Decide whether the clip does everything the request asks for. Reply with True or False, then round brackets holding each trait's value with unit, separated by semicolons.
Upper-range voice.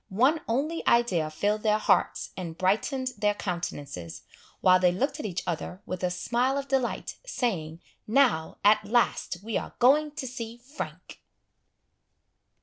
True (215 Hz)